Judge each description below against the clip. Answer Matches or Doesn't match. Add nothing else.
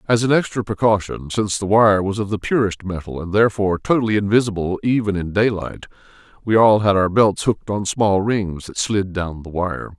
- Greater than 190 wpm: Matches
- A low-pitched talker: Matches